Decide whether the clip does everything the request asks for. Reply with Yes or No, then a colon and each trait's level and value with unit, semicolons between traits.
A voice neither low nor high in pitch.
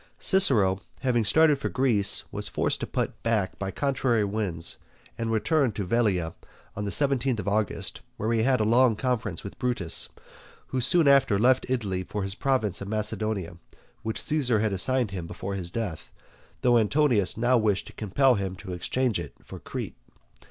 No: low, 110 Hz